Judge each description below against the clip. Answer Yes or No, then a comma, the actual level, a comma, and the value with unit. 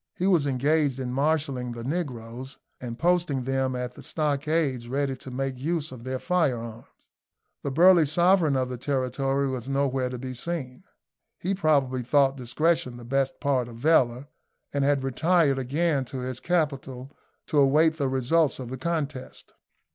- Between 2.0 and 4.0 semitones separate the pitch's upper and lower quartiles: Yes, average, 3.5 semitones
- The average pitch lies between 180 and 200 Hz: No, low, 135 Hz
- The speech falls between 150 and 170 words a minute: Yes, average, 160 wpm